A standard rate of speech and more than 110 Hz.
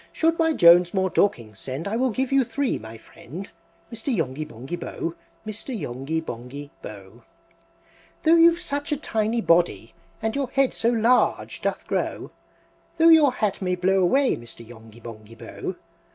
Yes: average, 165 wpm; high, 190 Hz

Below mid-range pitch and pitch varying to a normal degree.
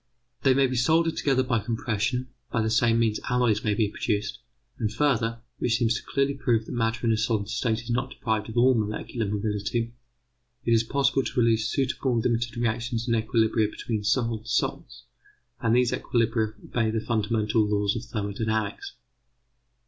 No: low, 115 Hz; narrow, 2.0 semitones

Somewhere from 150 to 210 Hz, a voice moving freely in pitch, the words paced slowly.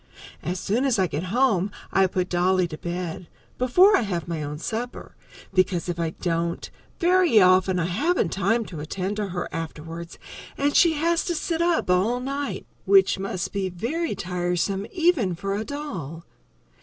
No: high, 190 Hz; wide, 6.8 semitones; average, 170 wpm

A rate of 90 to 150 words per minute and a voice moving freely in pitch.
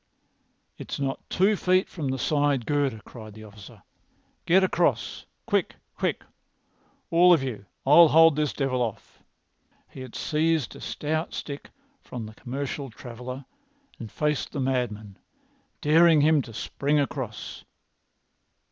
No: slow, 135 wpm; average, 4.3 semitones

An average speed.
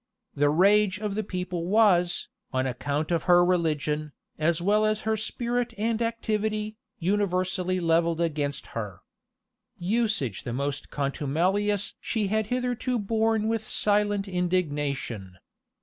No: slow, 125 wpm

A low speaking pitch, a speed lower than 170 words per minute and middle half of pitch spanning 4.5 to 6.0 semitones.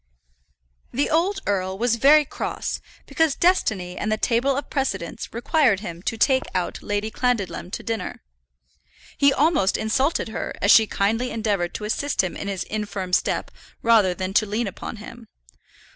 No: high, 220 Hz; average, 160 wpm; average, 4.9 semitones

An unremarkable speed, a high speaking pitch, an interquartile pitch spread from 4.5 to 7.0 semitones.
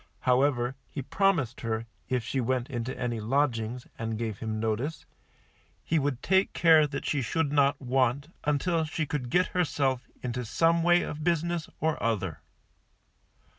No: average, 150 wpm; low, 135 Hz; average, 4.8 semitones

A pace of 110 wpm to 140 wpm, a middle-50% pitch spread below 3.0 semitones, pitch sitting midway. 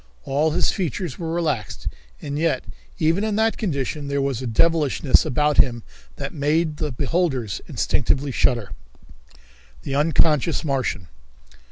No: slow, 135 wpm; average, 3.7 semitones; medium, 145 Hz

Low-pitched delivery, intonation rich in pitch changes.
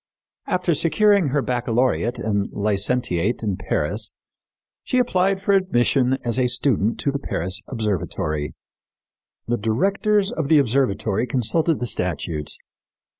Yes: low, 125 Hz; wide, 7.6 semitones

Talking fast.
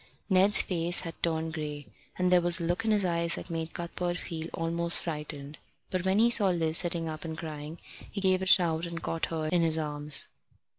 Yes: fast, 210 wpm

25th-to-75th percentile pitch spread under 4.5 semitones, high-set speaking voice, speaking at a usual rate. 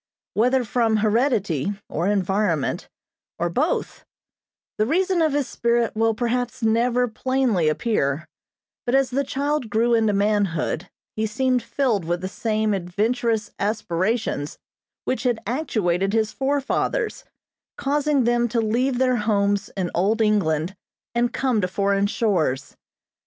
No: average, 3.9 semitones; high, 220 Hz; slow, 130 wpm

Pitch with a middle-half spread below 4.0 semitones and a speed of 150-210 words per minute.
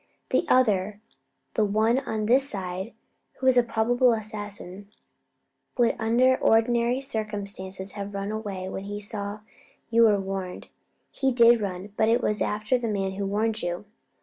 Yes: average, 2.8 semitones; average, 155 wpm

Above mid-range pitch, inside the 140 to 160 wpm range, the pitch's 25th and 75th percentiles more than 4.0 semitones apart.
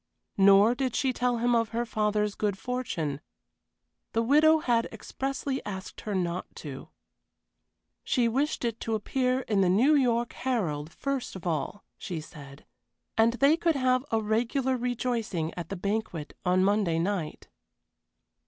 Yes: high, 225 Hz; average, 150 wpm; average, 5.1 semitones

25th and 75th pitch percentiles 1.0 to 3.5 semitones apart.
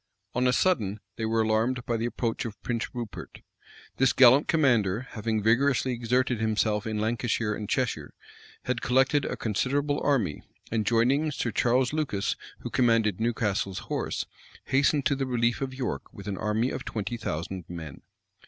Yes: average, 3.1 semitones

